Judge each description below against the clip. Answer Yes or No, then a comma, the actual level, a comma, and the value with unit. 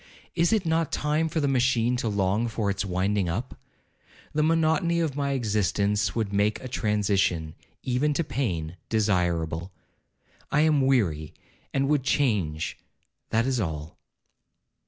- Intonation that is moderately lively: No, wide, 6.7 semitones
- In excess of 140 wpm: No, slow, 135 wpm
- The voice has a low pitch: Yes, low, 115 Hz